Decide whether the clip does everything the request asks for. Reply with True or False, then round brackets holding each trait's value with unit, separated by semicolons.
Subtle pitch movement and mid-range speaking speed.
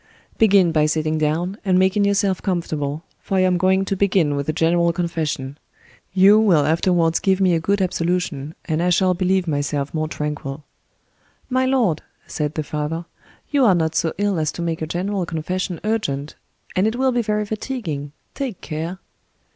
False (3.8 semitones; 170 wpm)